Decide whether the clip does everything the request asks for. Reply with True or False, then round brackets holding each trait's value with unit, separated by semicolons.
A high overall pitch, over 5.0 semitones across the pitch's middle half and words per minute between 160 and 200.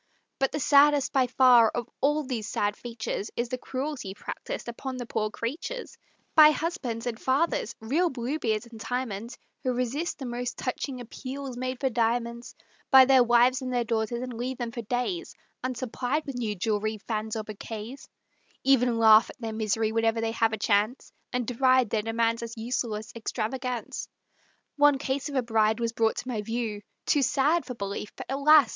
False (245 Hz; 2.8 semitones; 180 wpm)